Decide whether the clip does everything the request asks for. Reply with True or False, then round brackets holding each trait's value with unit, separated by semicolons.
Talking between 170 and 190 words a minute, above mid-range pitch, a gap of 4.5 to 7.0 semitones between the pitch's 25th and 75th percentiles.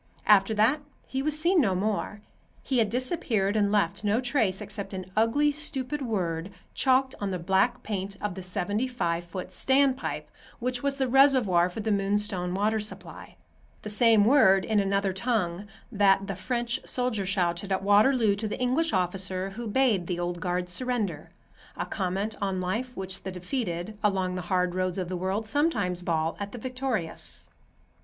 True (175 wpm; 205 Hz; 4.8 semitones)